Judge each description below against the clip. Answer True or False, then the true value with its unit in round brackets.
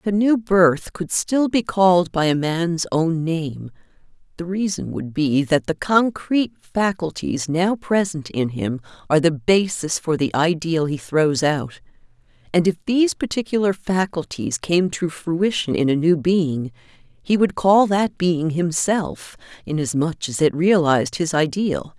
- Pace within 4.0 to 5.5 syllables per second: True (4.2 syllables/s)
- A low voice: False (170 Hz)